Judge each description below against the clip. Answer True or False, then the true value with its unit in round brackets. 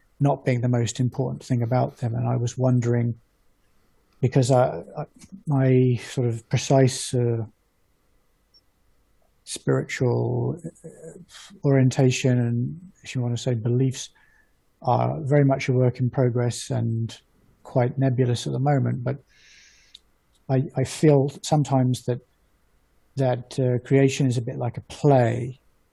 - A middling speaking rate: False (125 wpm)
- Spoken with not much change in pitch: True (2.0 semitones)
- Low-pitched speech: True (125 Hz)